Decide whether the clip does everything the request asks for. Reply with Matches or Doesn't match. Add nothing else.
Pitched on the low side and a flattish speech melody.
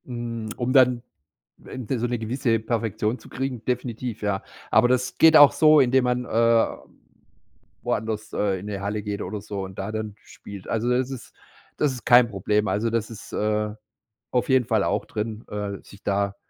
Doesn't match